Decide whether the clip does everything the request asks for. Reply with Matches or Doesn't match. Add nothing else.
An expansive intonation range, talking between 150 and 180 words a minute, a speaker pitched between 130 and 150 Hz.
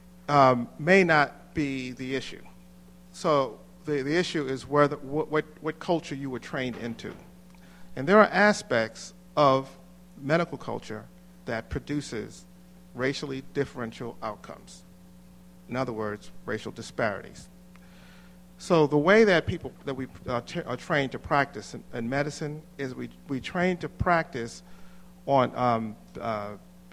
Doesn't match